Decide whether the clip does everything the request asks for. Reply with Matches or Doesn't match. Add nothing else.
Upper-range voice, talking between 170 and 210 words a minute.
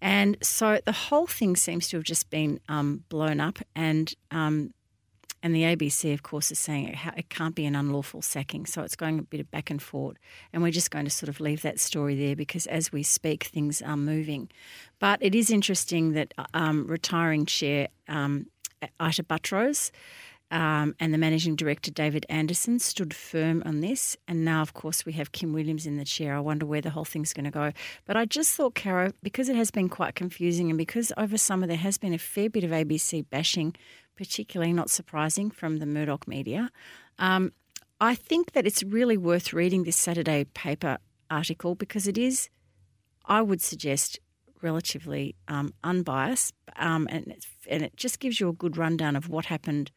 Doesn't match